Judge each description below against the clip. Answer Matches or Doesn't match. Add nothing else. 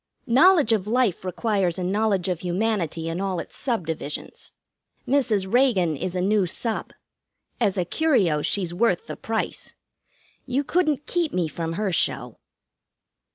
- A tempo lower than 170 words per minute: Matches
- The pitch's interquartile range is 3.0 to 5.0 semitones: Doesn't match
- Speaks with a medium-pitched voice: Doesn't match